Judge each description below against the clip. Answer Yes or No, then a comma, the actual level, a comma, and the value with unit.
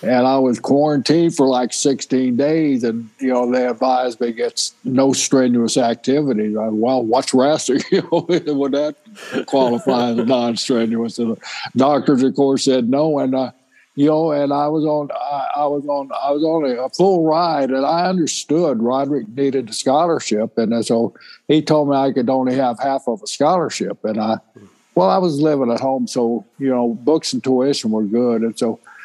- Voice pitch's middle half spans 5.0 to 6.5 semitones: No, average, 3.4 semitones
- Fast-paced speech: No, average, 195 wpm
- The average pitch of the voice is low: Yes, low, 130 Hz